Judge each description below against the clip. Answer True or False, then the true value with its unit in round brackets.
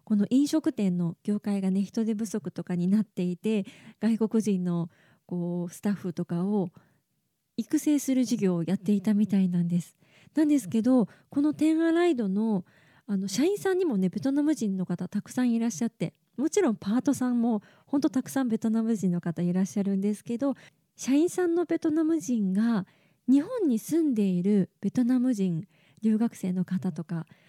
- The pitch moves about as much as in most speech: False (5.7 semitones)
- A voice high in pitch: True (210 Hz)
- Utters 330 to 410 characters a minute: True (350 characters per minute)